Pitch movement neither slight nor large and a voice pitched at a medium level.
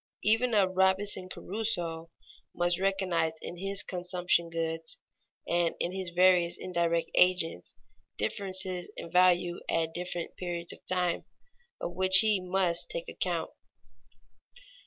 No: narrow, 1.8 semitones; medium, 180 Hz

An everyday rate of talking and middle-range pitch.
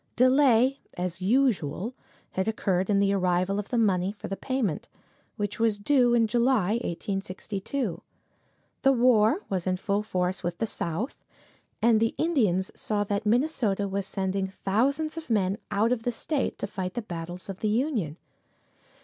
No: average, 160 wpm; high, 210 Hz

